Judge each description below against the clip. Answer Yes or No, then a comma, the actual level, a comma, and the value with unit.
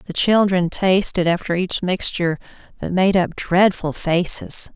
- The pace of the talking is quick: No, average, 140 wpm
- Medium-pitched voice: Yes, medium, 180 Hz